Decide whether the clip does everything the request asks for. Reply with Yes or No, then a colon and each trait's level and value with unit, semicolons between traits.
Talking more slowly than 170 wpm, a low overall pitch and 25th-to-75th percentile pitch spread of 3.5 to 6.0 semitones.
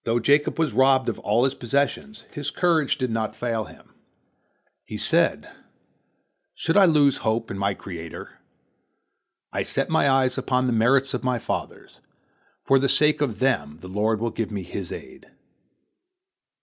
Yes: average, 160 wpm; low, 125 Hz; average, 4.1 semitones